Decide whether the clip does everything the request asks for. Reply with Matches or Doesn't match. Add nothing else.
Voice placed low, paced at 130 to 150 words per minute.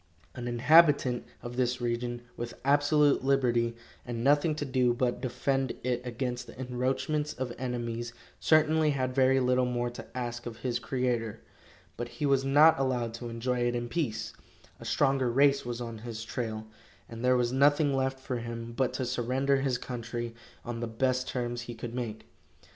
Doesn't match